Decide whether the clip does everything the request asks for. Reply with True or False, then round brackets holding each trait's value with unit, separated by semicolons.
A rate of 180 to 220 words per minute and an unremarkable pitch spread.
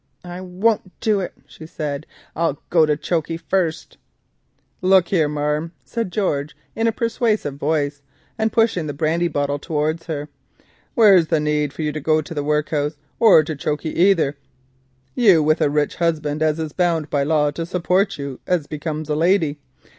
False (170 wpm; 3.3 semitones)